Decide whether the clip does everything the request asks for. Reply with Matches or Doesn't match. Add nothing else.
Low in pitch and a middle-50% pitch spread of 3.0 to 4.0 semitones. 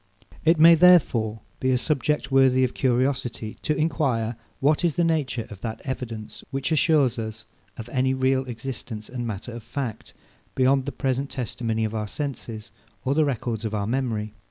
Matches